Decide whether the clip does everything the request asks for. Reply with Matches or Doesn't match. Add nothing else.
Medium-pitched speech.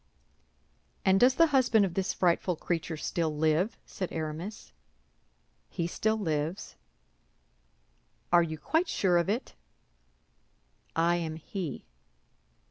Matches